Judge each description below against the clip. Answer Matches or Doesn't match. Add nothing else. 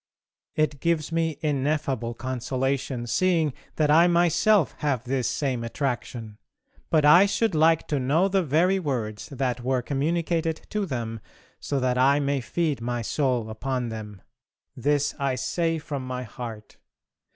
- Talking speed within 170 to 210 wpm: Doesn't match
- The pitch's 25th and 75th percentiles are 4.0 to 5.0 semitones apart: Matches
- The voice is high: Doesn't match